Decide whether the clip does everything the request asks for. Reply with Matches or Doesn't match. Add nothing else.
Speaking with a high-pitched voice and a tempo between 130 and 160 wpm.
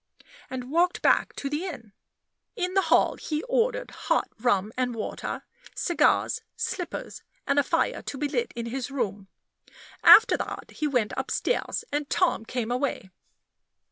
Matches